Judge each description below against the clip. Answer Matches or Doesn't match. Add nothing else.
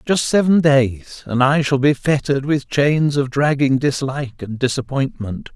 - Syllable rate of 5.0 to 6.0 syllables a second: Doesn't match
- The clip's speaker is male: Matches